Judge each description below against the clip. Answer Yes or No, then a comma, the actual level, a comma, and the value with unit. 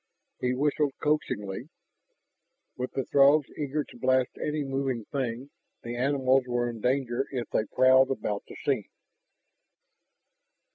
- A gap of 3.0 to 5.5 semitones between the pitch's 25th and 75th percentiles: No, narrow, 2.4 semitones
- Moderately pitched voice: No, low, 130 Hz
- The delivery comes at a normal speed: No, slow, 130 wpm